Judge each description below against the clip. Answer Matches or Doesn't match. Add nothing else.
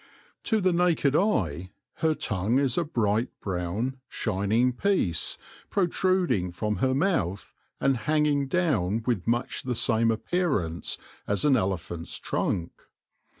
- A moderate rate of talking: Doesn't match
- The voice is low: Matches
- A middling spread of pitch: Doesn't match